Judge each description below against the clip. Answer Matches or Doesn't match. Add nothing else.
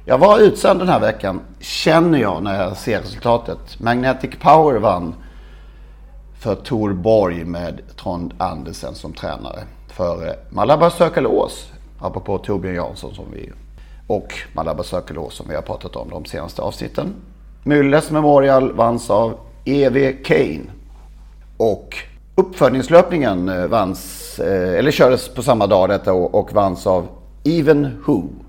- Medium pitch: Doesn't match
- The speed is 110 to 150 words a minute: Matches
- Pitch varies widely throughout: Matches